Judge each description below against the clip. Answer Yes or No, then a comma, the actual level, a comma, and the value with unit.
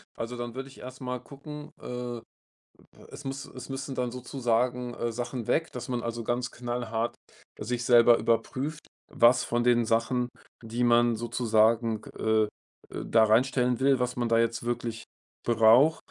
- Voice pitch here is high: No, low, 120 Hz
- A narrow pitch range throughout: Yes, narrow, 1.5 semitones